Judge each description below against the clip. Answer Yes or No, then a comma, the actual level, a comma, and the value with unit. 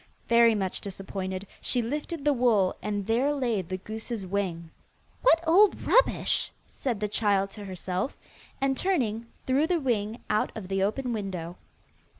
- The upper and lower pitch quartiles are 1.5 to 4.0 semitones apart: No, average, 5.2 semitones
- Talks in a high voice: Yes, high, 215 Hz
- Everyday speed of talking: Yes, average, 155 wpm